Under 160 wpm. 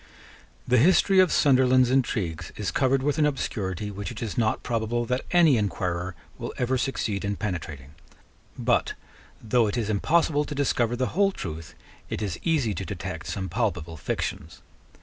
No: average, 165 wpm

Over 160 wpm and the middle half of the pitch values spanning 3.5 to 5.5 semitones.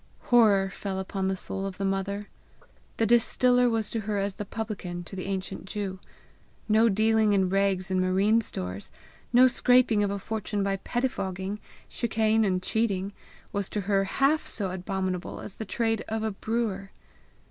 No: average, 170 wpm; narrow, 2.5 semitones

